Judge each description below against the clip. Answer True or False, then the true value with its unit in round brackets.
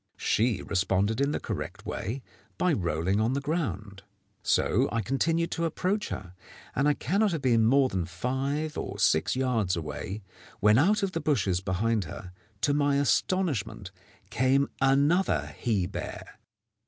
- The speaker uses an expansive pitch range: True (7.1 semitones)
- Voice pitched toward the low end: True (125 Hz)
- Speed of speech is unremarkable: True (155 wpm)